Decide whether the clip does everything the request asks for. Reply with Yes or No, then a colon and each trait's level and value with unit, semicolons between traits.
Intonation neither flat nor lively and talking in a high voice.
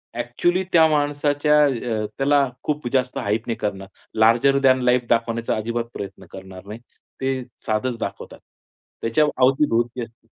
No: average, 3.5 semitones; low, 120 Hz